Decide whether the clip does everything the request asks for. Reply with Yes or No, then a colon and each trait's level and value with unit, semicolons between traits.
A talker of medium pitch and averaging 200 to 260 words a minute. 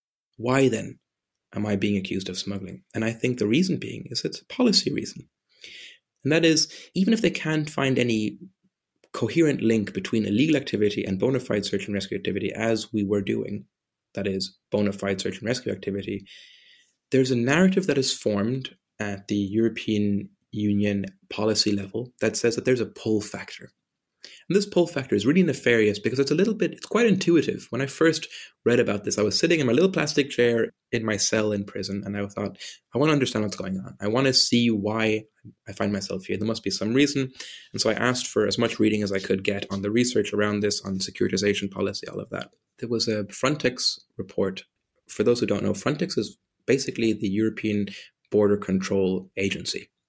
No: low, 110 Hz; fast, 205 wpm